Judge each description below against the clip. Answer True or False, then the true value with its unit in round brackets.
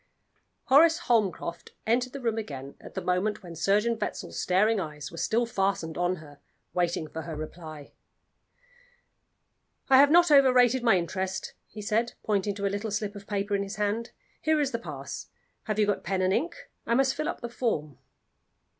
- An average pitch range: True (4.8 semitones)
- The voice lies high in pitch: True (205 Hz)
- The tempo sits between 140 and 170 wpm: False (180 wpm)